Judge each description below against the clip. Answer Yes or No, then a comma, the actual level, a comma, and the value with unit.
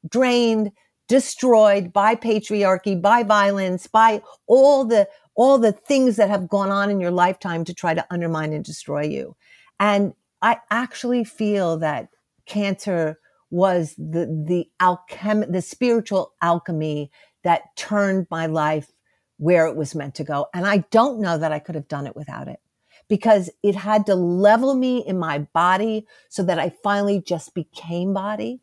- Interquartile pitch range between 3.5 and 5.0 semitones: Yes, average, 4.3 semitones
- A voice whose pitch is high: Yes, high, 195 Hz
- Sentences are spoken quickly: No, average, 160 wpm